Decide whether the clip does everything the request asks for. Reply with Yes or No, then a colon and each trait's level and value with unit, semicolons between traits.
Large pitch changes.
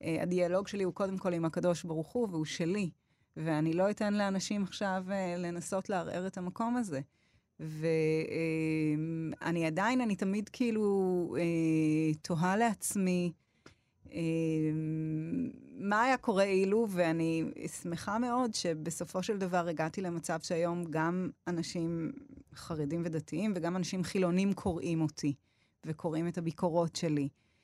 No: average, 3.3 semitones